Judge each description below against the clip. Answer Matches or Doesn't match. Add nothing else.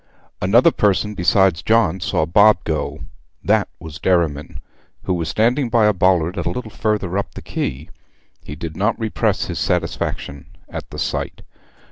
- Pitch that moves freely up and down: Doesn't match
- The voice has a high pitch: Doesn't match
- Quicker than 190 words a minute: Doesn't match